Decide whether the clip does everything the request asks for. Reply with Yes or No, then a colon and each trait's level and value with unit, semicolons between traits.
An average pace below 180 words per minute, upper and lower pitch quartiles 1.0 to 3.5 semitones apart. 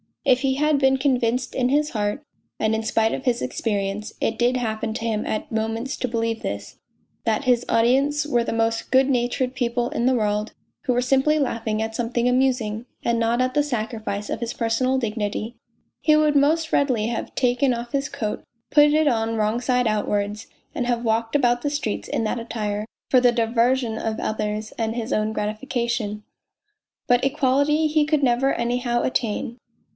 No: average, 190 wpm; average, 3.0 semitones